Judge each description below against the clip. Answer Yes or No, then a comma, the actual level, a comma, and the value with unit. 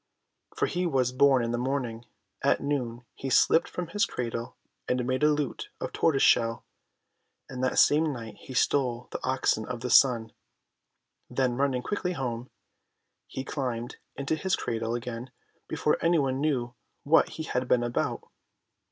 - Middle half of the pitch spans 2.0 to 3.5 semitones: Yes, average, 3.2 semitones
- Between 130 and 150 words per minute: No, average, 160 wpm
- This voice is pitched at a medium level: No, low, 130 Hz